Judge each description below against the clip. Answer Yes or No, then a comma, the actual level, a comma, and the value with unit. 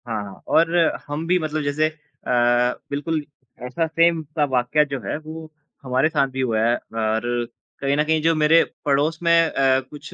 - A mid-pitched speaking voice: Yes, medium, 145 Hz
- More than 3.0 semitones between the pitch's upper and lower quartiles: Yes, average, 3.9 semitones